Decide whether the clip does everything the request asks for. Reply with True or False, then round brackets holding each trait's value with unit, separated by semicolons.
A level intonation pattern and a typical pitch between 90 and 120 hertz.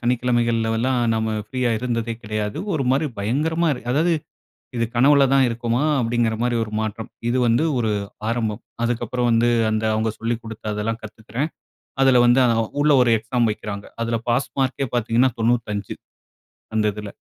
True (2.1 semitones; 115 Hz)